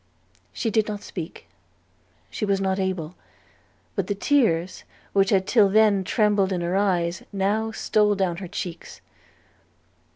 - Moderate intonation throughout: No, narrow, 2.3 semitones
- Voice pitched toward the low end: No, high, 195 Hz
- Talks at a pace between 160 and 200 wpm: No, average, 140 wpm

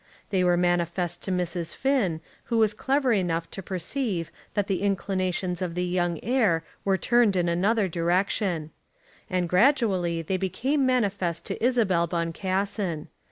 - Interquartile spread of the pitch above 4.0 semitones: No, average, 3.3 semitones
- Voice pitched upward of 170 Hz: Yes, medium, 185 Hz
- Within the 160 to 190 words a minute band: No, average, 145 wpm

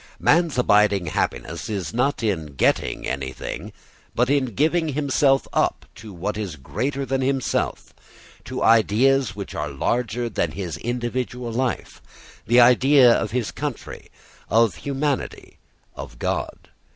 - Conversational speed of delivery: No, slow, 130 wpm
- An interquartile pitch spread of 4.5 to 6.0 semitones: Yes, average, 5.1 semitones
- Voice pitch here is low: Yes, low, 120 Hz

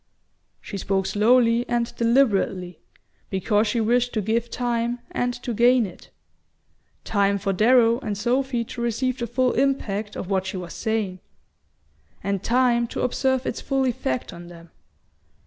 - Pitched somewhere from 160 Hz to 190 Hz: No, high, 230 Hz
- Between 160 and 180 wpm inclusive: No, average, 150 wpm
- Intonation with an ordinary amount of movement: Yes, average, 3.7 semitones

